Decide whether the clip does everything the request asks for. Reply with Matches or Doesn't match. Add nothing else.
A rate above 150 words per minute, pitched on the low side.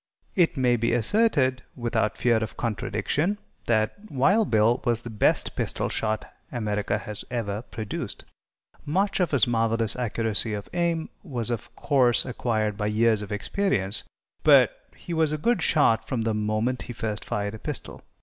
Matches